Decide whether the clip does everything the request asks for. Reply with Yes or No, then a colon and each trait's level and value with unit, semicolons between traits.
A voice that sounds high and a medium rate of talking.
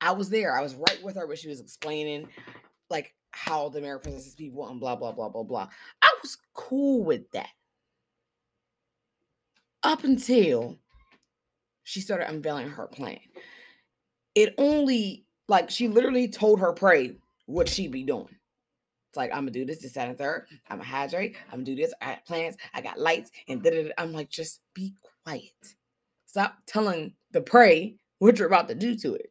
Yes: high, 200 Hz; average, 180 wpm